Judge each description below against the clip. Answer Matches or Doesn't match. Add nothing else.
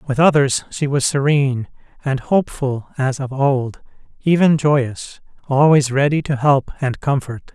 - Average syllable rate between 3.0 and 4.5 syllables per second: Matches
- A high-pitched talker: Doesn't match